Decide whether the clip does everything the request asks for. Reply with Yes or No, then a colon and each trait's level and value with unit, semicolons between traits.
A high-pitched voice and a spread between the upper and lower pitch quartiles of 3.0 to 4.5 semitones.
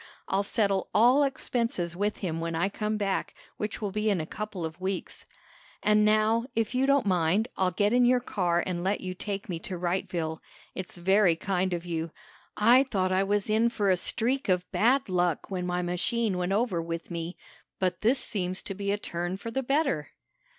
Yes: high, 195 Hz; average, 3.4 semitones